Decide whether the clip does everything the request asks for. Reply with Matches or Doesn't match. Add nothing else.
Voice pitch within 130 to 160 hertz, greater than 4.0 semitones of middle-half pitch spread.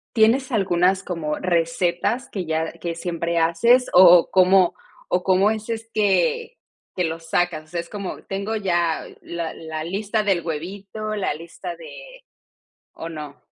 Doesn't match